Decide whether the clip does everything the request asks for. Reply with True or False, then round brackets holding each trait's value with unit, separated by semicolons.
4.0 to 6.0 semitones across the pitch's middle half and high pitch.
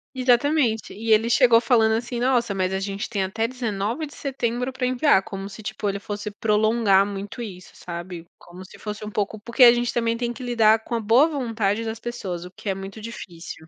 False (3.3 semitones; 220 Hz)